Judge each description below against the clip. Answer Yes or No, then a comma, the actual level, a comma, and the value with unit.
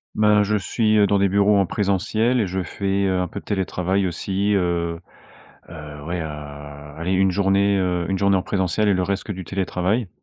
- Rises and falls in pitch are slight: Yes, narrow, 2.3 semitones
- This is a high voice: No, very low, 95 Hz